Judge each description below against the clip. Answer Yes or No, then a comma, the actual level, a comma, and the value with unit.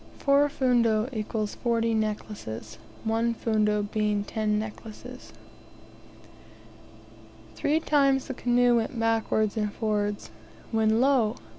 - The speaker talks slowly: Yes, slow, 105 wpm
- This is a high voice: Yes, high, 220 Hz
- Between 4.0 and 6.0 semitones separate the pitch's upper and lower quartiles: No, narrow, 2.5 semitones